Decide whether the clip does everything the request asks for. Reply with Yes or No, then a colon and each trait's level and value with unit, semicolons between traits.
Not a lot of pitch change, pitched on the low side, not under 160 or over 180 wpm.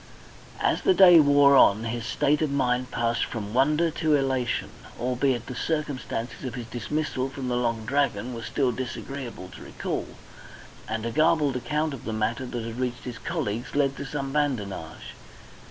No: average, 3.5 semitones; low, 130 Hz; average, 170 wpm